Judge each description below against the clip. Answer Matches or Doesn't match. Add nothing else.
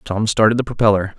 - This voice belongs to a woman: Doesn't match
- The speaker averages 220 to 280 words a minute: Doesn't match